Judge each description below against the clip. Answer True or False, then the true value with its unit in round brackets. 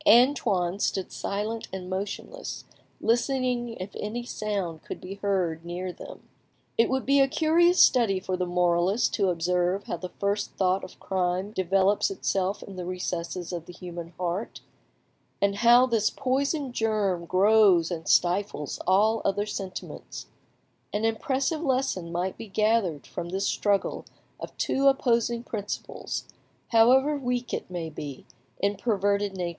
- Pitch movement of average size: True (4.4 semitones)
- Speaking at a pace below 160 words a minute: True (145 wpm)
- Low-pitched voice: False (200 Hz)